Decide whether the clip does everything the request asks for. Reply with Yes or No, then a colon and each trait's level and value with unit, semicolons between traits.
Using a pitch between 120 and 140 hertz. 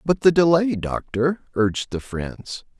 Yes: low, 135 Hz